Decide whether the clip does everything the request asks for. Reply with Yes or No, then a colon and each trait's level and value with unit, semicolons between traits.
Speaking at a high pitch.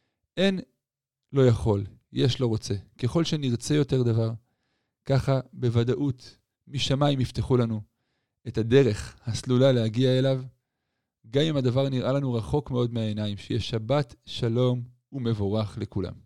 No: low, 125 Hz